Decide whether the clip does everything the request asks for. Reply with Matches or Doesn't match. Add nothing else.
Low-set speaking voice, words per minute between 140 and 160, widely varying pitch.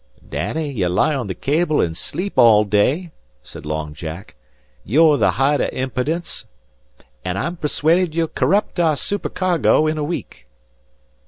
Doesn't match